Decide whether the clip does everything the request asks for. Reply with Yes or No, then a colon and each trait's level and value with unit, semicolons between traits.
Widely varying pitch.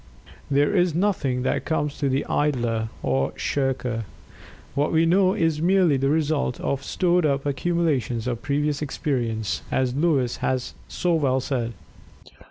No: average, 4.2 semitones